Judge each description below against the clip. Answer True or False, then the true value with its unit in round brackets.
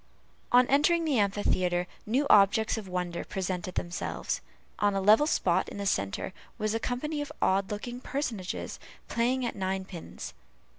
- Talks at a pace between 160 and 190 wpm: False (150 wpm)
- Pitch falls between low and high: False (205 Hz)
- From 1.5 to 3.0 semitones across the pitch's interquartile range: False (4.9 semitones)